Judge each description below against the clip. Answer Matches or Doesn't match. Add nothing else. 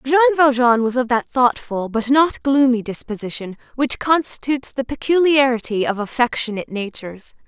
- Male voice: Doesn't match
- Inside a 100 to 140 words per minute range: Matches